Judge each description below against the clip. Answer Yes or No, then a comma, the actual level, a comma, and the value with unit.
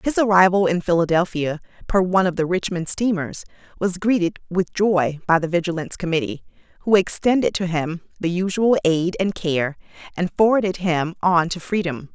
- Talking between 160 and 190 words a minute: Yes, average, 165 wpm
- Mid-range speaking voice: Yes, medium, 180 Hz